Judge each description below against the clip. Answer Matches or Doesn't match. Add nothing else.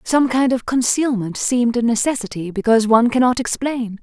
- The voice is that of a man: Doesn't match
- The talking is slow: Doesn't match